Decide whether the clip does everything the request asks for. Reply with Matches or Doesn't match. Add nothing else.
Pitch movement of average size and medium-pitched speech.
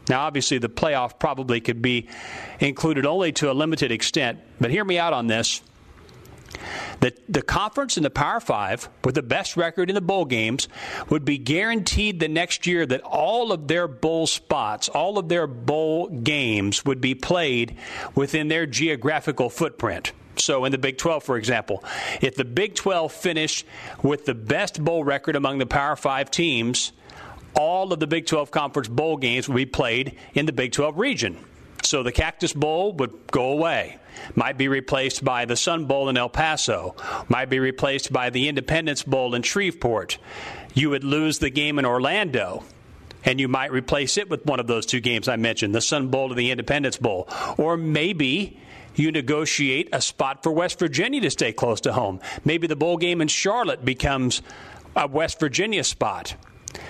Matches